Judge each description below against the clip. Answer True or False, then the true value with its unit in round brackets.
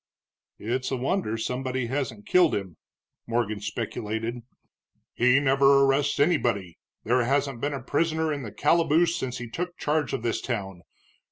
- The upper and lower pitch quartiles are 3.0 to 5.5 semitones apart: True (4.0 semitones)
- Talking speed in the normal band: True (150 wpm)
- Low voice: True (130 Hz)